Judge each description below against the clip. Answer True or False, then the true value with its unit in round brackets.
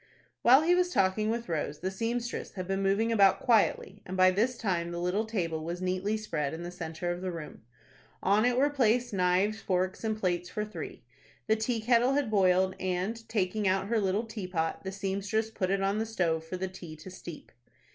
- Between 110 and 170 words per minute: False (205 wpm)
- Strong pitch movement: False (3.5 semitones)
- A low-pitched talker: False (195 Hz)